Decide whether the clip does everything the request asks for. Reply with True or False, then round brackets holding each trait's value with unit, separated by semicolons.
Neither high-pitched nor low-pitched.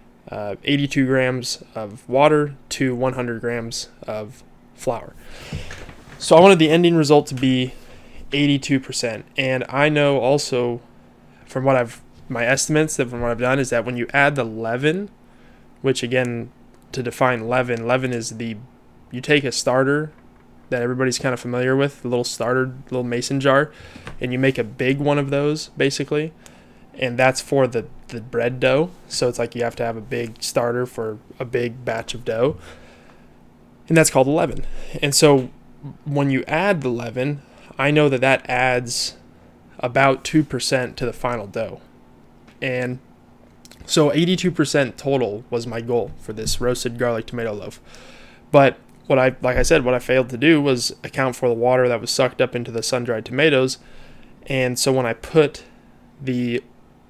False (125 Hz)